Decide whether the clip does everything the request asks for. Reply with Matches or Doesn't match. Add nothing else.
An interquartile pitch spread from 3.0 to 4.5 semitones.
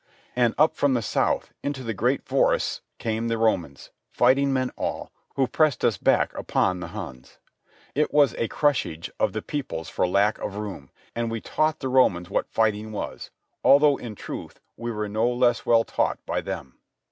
Matches